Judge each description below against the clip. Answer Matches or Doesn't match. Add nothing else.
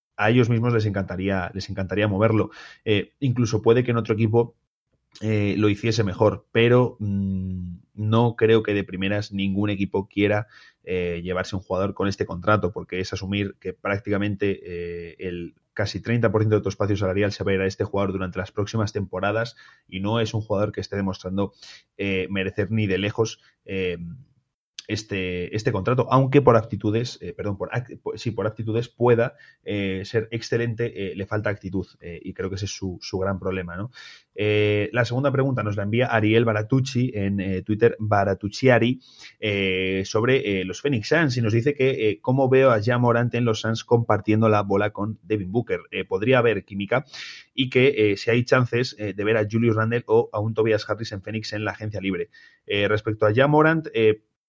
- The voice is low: Matches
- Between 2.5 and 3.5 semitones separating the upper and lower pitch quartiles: Matches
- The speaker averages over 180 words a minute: Matches